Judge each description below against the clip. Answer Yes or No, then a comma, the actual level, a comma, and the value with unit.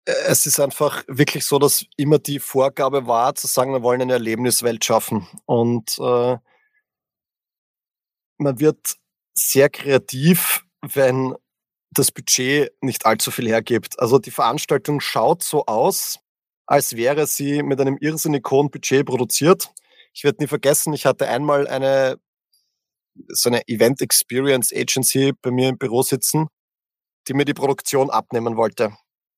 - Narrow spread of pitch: Yes, narrow, 2.2 semitones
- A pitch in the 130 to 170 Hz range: Yes, low, 135 Hz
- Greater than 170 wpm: No, average, 140 wpm